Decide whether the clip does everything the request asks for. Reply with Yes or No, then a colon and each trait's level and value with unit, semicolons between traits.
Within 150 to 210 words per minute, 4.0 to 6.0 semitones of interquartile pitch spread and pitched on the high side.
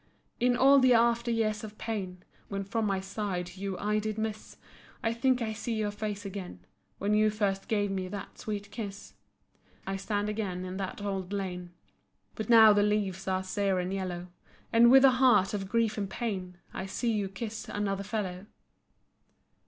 No: average, 180 wpm; narrow, 2.4 semitones; high, 205 Hz